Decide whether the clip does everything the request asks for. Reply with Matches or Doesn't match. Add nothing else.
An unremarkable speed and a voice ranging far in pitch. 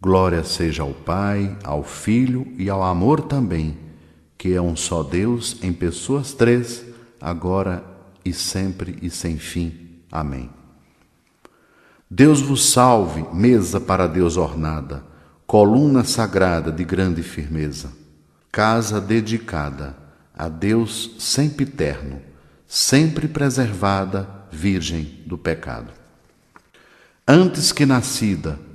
Doesn't match